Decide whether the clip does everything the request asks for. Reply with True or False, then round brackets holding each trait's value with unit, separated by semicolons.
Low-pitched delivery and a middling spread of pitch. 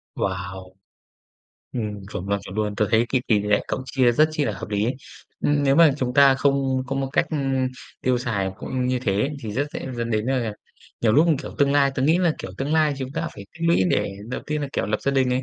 True (130 Hz; 4.6 semitones)